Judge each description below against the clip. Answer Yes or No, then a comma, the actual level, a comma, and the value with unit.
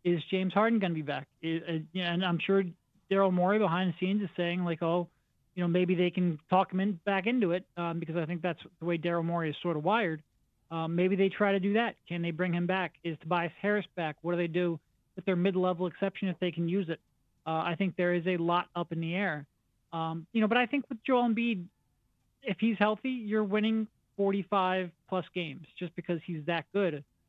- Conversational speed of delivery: No, fast, 235 wpm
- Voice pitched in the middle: Yes, medium, 180 Hz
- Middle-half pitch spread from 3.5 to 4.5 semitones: No, narrow, 2.6 semitones